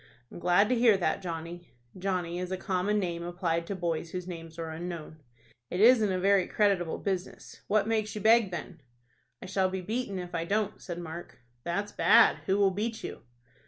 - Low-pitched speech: No, medium, 185 Hz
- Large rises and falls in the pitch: No, average, 3.0 semitones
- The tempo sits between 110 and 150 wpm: No, average, 195 wpm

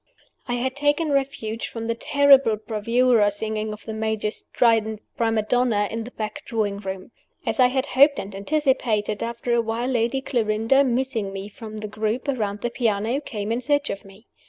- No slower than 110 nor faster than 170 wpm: No, average, 180 wpm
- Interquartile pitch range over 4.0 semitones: No, average, 3.4 semitones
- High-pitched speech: Yes, high, 230 Hz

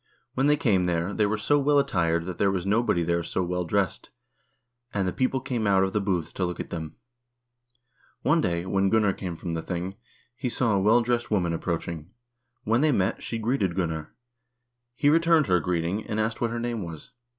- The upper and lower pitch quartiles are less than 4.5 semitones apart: No, average, 5.2 semitones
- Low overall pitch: Yes, low, 100 Hz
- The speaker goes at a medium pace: No, fast, 215 wpm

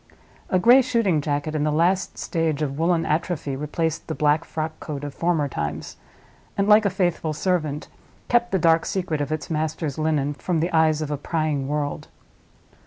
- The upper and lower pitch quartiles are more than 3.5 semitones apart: No, average, 2.8 semitones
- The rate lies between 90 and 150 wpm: No, average, 175 wpm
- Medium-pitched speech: Yes, medium, 155 Hz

